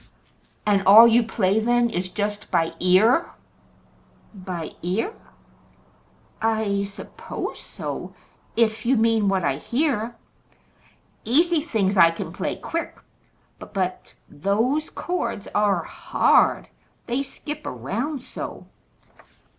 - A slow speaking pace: Yes, slow, 110 wpm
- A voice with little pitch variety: No, average, 3.9 semitones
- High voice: Yes, high, 220 Hz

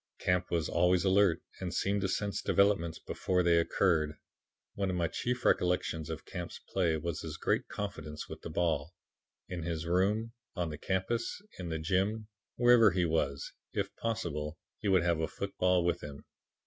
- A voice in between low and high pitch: No, very low, 90 Hz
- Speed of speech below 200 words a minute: Yes, average, 175 wpm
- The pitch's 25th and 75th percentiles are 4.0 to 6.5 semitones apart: No, average, 3.4 semitones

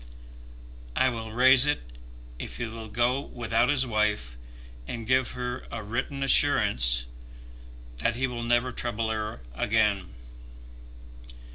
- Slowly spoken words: Yes, slow, 125 wpm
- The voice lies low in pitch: Yes, low, 120 Hz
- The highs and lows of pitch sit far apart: No, average, 2.8 semitones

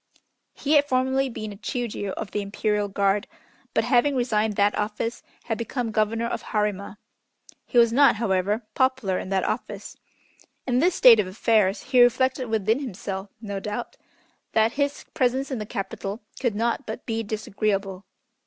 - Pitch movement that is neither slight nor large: Yes, average, 3.5 semitones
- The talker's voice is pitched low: No, high, 220 Hz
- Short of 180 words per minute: Yes, average, 160 wpm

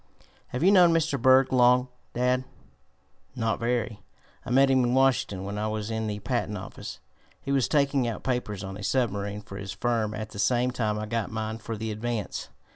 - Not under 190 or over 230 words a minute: Yes, average, 200 wpm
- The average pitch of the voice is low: Yes, low, 115 Hz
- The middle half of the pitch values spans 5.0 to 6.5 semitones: No, average, 3.2 semitones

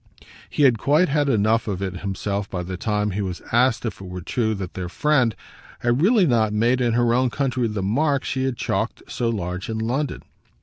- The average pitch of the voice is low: Yes, low, 115 Hz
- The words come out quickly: Yes, fast, 215 wpm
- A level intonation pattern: No, average, 4.7 semitones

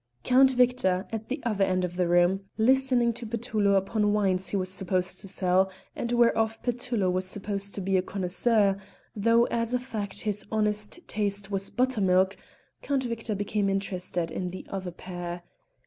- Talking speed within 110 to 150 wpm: No, average, 170 wpm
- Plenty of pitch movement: No, average, 3.6 semitones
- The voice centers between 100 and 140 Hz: No, high, 200 Hz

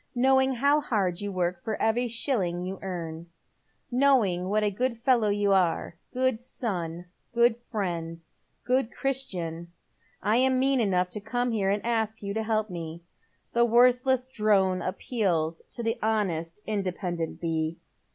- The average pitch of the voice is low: No, high, 210 Hz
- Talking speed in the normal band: Yes, average, 160 wpm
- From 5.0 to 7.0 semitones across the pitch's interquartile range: Yes, wide, 5.4 semitones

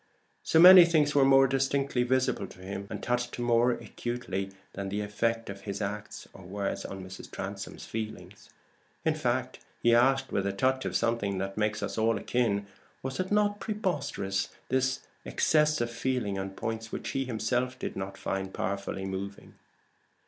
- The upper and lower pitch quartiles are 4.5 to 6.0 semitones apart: Yes, average, 4.9 semitones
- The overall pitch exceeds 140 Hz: No, low, 115 Hz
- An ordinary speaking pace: Yes, average, 170 wpm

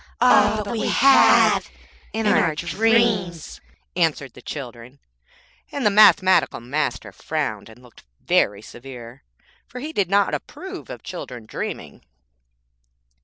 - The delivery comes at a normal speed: No, slow, 120 wpm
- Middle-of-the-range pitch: Yes, medium, 175 Hz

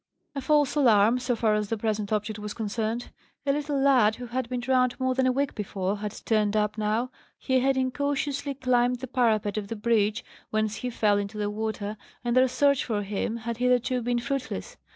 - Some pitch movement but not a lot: Yes, average, 3.3 semitones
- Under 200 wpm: No, fast, 205 wpm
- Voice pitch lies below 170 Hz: No, high, 235 Hz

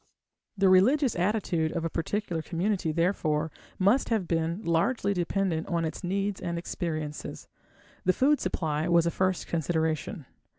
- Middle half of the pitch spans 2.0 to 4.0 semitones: Yes, average, 3.4 semitones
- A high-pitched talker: No, medium, 175 Hz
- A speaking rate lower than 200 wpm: Yes, average, 140 wpm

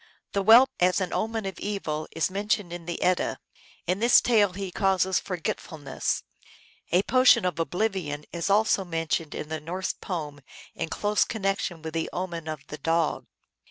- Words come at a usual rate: Yes, average, 165 wpm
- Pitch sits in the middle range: Yes, medium, 180 Hz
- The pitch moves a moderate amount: Yes, average, 3.5 semitones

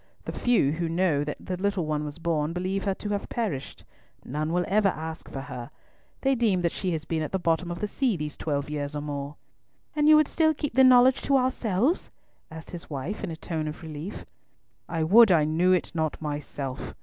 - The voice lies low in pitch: No, medium, 170 Hz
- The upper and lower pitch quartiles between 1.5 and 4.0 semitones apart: No, average, 5.3 semitones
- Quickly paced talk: Yes, fast, 220 wpm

